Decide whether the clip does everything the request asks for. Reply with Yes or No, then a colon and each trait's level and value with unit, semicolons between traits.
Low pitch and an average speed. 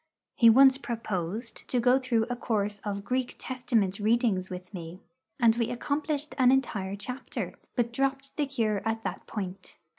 No: high, 230 Hz; average, 160 wpm